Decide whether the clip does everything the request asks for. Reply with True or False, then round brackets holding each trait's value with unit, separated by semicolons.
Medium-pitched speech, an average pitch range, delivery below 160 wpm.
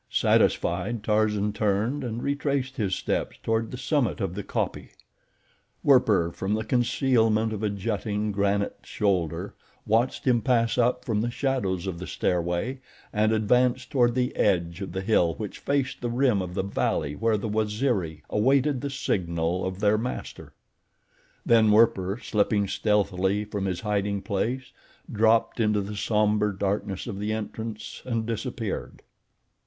False (105 Hz; 3.2 semitones; 150 wpm)